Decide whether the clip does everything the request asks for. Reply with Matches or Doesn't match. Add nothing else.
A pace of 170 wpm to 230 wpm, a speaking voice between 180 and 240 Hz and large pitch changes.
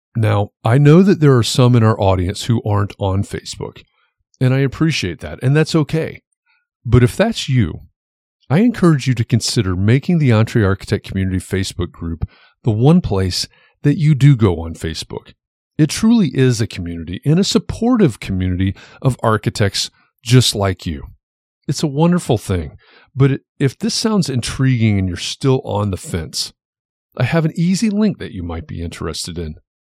Doesn't match